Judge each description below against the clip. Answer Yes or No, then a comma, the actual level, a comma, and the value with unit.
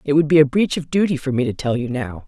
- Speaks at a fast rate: Yes, fast, 345 wpm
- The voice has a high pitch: No, medium, 140 Hz